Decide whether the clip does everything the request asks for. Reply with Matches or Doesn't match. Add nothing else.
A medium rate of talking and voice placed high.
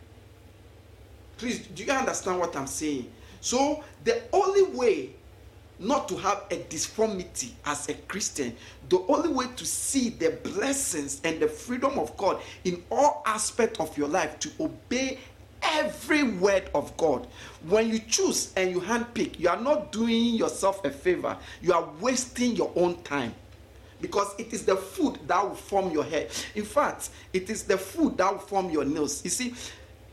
Matches